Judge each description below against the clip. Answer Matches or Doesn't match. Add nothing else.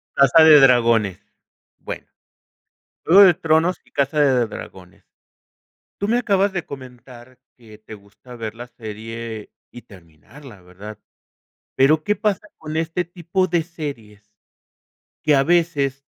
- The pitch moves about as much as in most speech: Doesn't match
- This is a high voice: Doesn't match